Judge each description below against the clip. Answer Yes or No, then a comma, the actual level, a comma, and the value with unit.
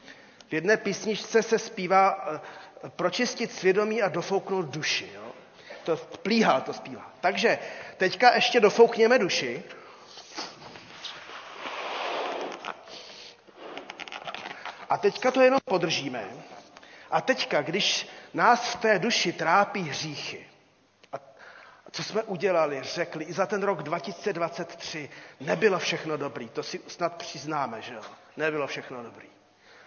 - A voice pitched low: No, high, 190 Hz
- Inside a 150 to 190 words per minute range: No, slow, 115 wpm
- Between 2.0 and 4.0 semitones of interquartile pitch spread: No, average, 5.3 semitones